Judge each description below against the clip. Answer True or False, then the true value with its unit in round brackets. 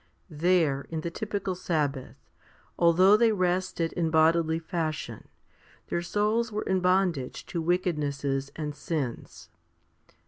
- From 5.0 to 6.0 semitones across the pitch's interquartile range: False (3.2 semitones)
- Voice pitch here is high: False (170 Hz)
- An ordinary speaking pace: False (115 wpm)